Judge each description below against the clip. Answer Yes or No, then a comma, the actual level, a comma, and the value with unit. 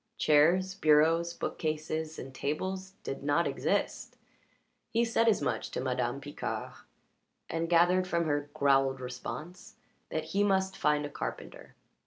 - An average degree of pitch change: Yes, average, 4.0 semitones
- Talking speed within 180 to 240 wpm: No, slow, 135 wpm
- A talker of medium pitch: Yes, medium, 160 Hz